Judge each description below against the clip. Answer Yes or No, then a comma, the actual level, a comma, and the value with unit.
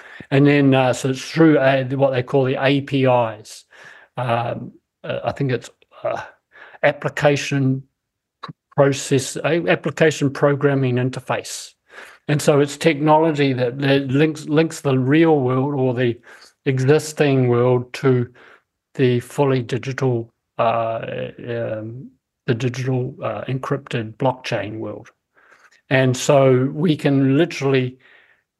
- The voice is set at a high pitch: No, low, 135 Hz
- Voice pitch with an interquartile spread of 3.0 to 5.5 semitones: No, narrow, 2.5 semitones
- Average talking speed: No, slow, 115 wpm